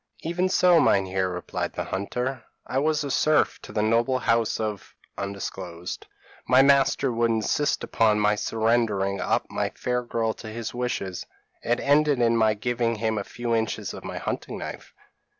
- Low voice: Yes, low, 115 Hz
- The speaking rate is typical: Yes, average, 170 wpm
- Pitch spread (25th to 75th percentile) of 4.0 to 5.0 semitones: No, average, 3.3 semitones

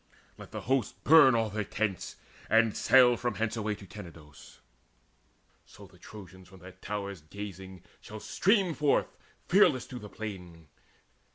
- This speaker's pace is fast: No, average, 150 wpm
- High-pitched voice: No, low, 105 Hz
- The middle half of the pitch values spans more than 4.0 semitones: Yes, average, 4.4 semitones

